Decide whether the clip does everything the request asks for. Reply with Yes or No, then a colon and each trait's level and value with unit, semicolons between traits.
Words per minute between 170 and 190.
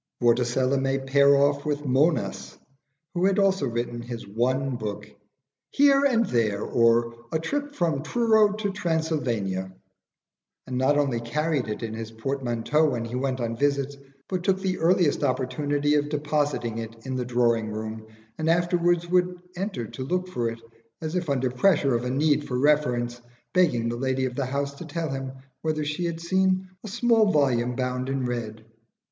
Yes: average, 175 wpm